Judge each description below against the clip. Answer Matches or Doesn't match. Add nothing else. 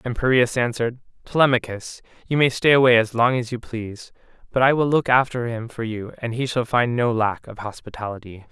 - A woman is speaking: Doesn't match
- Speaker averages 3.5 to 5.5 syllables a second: Doesn't match